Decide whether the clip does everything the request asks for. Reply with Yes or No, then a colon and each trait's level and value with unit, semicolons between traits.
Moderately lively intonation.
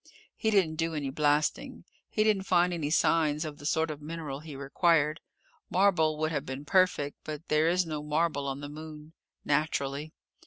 No: narrow, 2.2 semitones